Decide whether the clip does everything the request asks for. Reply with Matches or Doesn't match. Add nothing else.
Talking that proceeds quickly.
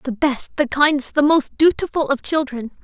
Doesn't match